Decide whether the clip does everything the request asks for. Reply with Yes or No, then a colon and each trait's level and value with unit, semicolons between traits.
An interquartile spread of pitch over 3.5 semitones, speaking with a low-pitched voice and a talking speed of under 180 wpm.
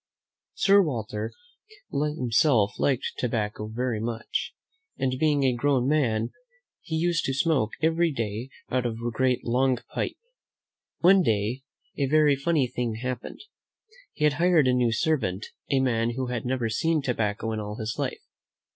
Yes: average, 4.5 semitones; low, 125 Hz; average, 155 wpm